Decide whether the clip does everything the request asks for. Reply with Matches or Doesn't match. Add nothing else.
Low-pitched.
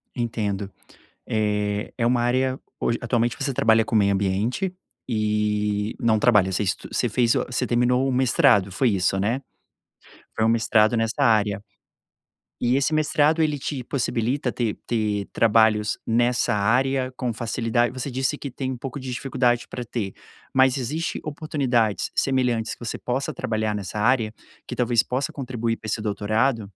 Matches